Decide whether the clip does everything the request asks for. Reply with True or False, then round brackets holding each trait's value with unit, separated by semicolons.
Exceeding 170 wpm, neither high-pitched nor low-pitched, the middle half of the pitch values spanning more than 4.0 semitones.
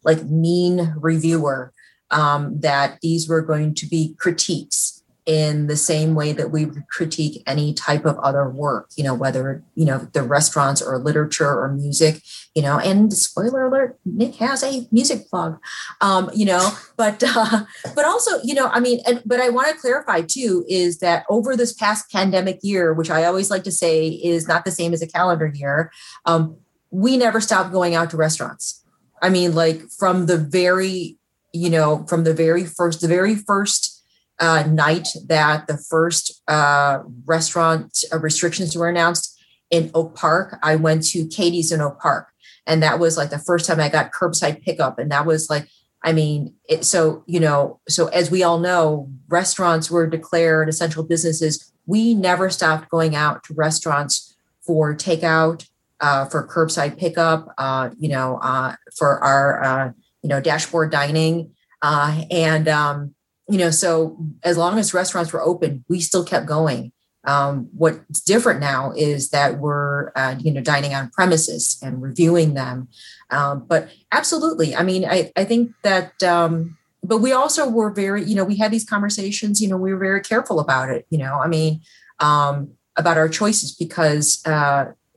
False (180 wpm; 165 Hz; 3.4 semitones)